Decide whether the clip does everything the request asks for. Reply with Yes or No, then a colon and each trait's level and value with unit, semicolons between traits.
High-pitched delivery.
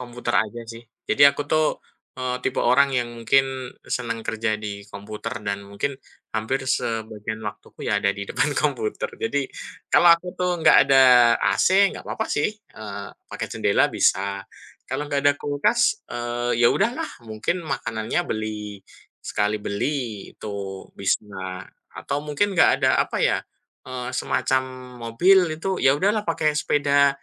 No: low, 125 Hz